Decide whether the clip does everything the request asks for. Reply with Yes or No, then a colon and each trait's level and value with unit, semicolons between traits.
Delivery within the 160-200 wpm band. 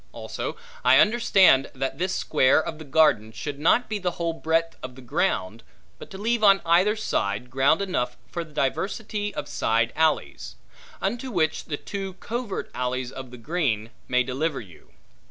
Yes: average, 170 wpm